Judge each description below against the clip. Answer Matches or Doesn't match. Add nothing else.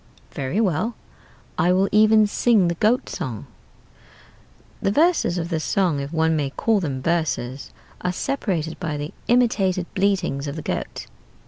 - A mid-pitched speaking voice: Matches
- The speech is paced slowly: Doesn't match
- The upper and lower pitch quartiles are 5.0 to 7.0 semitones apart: Matches